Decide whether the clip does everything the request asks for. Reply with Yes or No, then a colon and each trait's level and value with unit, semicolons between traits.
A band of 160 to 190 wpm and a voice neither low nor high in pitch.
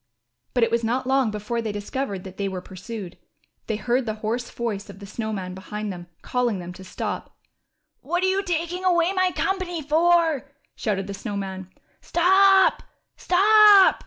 No: average, 180 wpm; high, 235 Hz